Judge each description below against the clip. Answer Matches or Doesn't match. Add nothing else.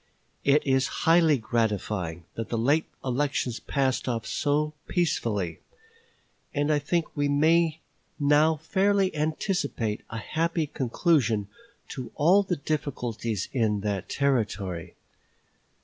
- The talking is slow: Matches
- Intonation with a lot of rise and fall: Matches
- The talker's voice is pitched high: Doesn't match